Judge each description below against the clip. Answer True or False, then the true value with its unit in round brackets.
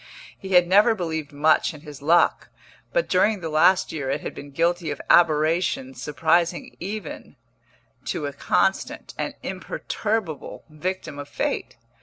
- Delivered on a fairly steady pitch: False (4.0 semitones)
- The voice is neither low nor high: True (160 Hz)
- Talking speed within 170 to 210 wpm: False (145 wpm)